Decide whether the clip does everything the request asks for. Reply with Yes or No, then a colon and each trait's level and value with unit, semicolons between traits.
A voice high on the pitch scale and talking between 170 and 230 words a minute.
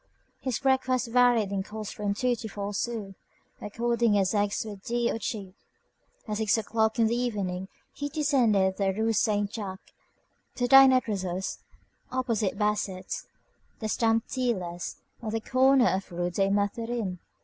No: high, 220 Hz; average, 160 wpm